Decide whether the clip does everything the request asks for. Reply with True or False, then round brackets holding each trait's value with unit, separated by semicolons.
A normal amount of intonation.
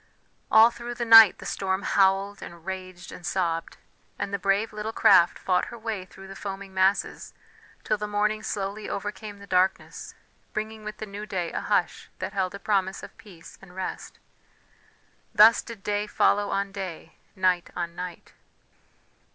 False (2.2 semitones)